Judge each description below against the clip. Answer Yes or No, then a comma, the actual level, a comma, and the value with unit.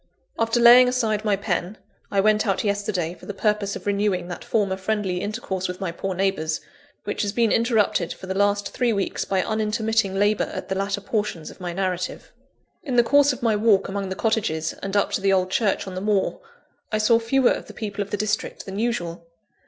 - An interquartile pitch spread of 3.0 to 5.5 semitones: No, narrow, 2.5 semitones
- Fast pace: Yes, fast, 215 wpm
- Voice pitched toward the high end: Yes, high, 205 Hz